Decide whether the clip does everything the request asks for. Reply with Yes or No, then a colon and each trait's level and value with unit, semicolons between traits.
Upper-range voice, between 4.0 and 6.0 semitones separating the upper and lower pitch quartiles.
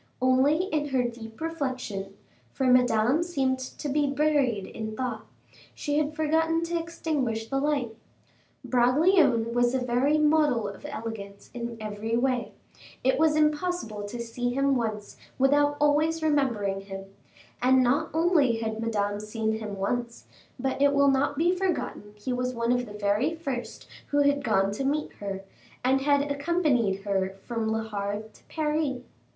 Yes: very high, 255 Hz; average, 4.9 semitones